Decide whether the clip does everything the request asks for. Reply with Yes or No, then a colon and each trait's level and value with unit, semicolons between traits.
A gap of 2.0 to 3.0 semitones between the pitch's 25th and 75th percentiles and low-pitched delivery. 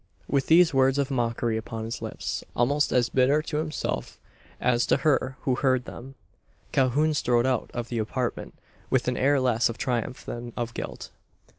Yes: narrow, 2.6 semitones; low, 130 Hz